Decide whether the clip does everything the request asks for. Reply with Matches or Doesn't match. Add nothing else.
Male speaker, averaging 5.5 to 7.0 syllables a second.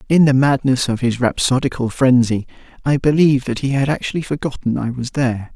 Matches